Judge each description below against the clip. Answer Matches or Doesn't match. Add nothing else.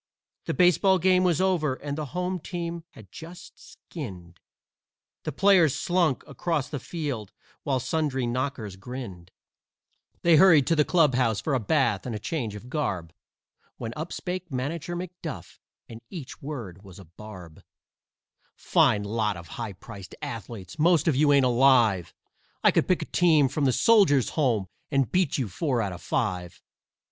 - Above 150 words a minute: Matches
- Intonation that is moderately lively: Doesn't match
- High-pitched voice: Doesn't match